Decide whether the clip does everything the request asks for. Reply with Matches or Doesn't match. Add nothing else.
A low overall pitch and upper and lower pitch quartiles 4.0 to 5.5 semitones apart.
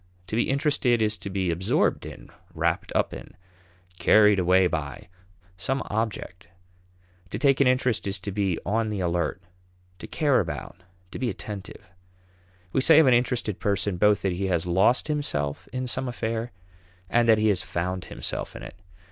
Matches